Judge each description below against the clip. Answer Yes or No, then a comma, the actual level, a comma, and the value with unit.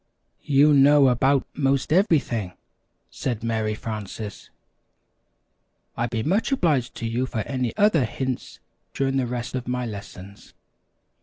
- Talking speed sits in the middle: No, slow, 130 wpm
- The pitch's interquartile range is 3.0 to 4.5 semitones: Yes, average, 3.6 semitones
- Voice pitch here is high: No, low, 125 Hz